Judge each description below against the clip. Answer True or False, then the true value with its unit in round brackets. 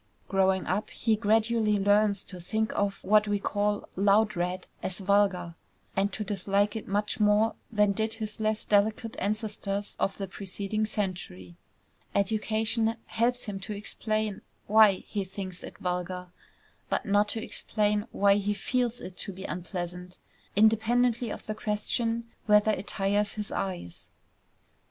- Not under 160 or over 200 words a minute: False (145 wpm)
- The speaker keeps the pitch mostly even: True (1.9 semitones)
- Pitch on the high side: True (205 Hz)